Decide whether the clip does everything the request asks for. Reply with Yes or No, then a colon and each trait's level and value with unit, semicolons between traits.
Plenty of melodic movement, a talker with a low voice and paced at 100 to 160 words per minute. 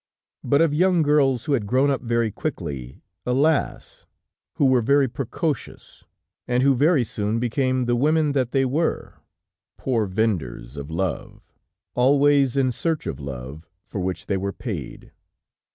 Yes: wide, 5.7 semitones; low, 125 Hz; average, 150 wpm